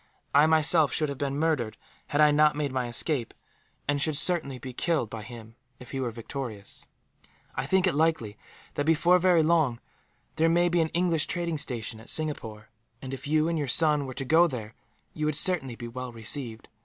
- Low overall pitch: No, medium, 145 Hz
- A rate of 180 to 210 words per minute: Yes, average, 200 wpm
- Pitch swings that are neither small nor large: Yes, average, 4.7 semitones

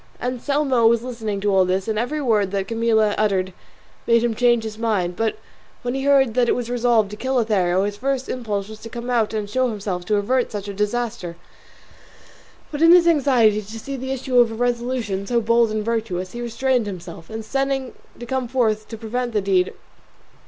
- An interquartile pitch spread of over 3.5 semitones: No, average, 3.2 semitones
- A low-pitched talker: No, high, 230 Hz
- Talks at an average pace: No, fast, 210 wpm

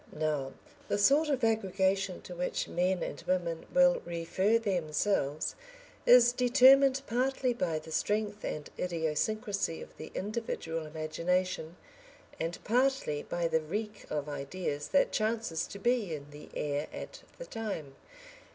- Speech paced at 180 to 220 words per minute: No, slow, 135 wpm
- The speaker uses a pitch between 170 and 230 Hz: Yes, medium, 185 Hz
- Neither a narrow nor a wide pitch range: No, wide, 6.1 semitones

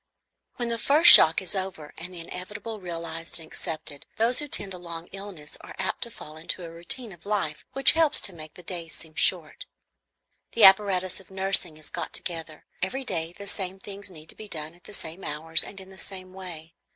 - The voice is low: No, medium, 185 Hz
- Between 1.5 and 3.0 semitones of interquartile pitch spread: No, average, 3.6 semitones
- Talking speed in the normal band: No, fast, 210 wpm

